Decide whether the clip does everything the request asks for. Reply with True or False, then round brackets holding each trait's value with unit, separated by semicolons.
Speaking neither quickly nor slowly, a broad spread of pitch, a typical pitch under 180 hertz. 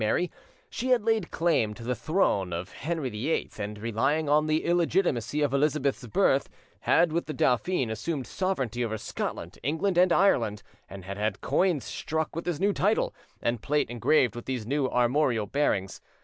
True (175 wpm; 6.6 semitones; 140 Hz)